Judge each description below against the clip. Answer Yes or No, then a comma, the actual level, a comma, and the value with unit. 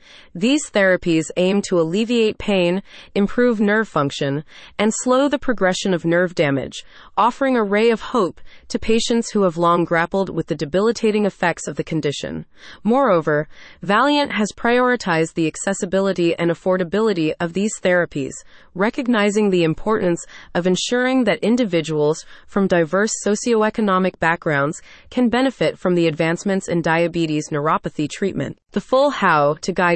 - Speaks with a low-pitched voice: No, high, 190 Hz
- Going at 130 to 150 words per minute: Yes, average, 140 wpm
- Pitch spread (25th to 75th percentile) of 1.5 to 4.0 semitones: No, average, 4.7 semitones